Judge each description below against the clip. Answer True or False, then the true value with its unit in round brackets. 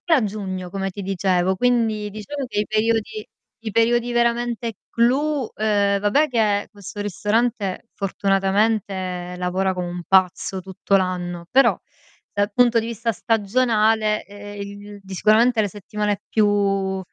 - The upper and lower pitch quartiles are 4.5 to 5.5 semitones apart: False (2.9 semitones)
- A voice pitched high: True (205 Hz)